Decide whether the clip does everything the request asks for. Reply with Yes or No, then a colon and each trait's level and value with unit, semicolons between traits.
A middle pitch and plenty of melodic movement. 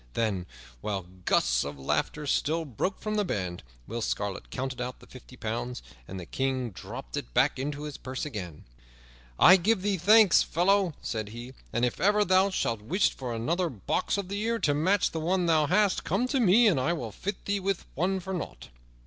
Yes: medium, 150 Hz; wide, 8.8 semitones